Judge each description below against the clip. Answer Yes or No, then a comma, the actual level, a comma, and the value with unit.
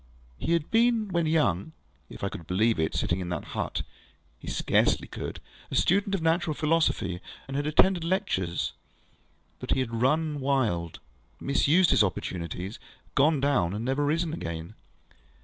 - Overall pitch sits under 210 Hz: Yes, medium, 140 Hz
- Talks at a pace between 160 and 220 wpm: No, average, 150 wpm